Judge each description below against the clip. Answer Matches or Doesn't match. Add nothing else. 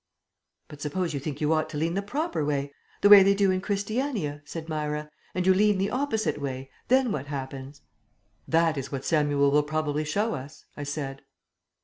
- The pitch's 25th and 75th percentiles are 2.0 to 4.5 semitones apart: Doesn't match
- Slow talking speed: Doesn't match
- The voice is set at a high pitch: Doesn't match